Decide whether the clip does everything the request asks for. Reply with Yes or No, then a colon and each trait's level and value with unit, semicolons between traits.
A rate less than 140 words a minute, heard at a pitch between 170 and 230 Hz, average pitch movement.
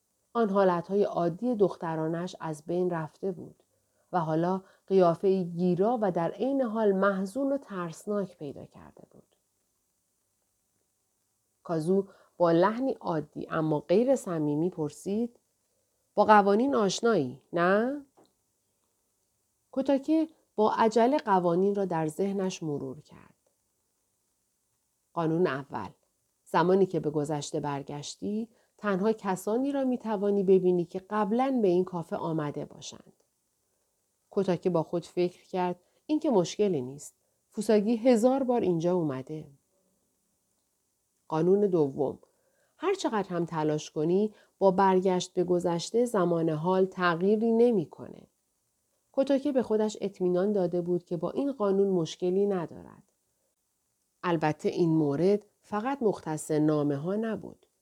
Yes: average, 115 wpm; medium, 185 Hz; average, 4.3 semitones